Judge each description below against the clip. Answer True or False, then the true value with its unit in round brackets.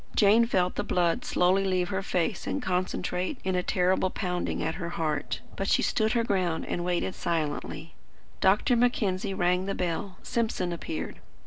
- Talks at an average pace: True (165 wpm)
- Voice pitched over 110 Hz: True (185 Hz)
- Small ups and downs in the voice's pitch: True (2.0 semitones)